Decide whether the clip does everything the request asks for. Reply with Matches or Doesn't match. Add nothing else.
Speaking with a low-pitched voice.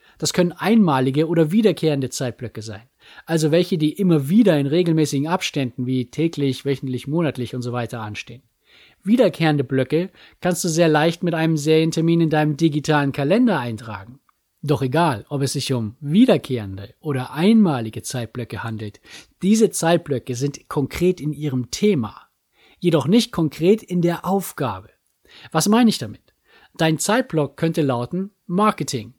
Doesn't match